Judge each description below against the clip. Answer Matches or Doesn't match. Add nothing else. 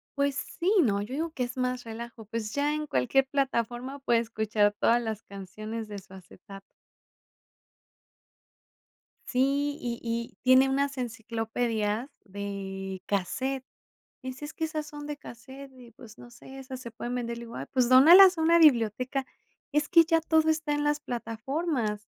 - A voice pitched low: Doesn't match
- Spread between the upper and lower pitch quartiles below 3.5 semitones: Doesn't match